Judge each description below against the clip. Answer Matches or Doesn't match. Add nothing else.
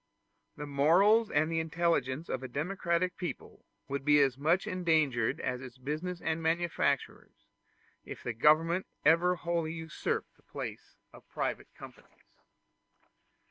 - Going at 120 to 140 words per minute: Matches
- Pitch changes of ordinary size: Matches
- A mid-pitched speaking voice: Matches